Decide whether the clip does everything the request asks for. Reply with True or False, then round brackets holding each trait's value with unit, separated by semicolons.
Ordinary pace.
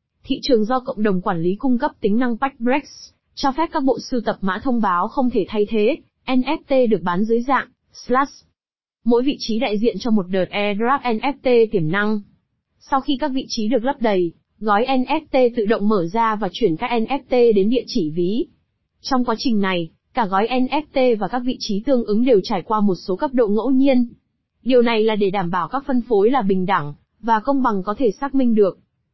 True (220 wpm)